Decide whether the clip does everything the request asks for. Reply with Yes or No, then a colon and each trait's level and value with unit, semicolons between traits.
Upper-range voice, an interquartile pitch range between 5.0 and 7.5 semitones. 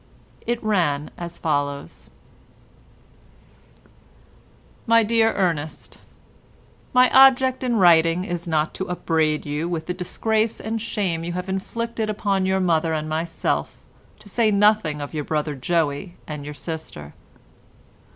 No: medium, 175 Hz; wide, 5.5 semitones